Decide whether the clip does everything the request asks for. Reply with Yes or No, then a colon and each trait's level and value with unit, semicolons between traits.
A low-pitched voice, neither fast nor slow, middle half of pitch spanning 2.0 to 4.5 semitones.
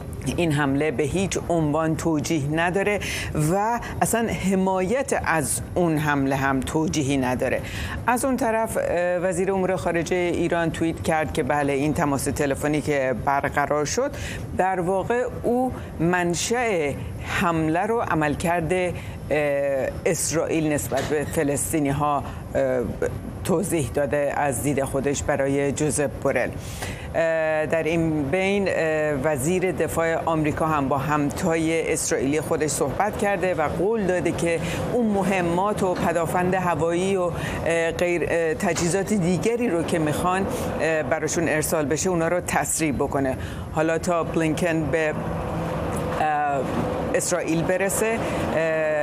No: medium, 165 Hz; average, 115 wpm; average, 3.5 semitones